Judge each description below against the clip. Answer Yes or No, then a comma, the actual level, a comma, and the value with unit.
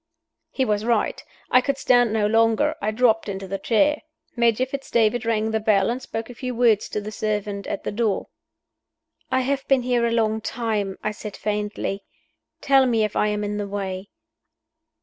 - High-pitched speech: Yes, high, 220 Hz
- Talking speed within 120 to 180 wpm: No, average, 190 wpm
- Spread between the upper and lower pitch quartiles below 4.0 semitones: Yes, average, 2.8 semitones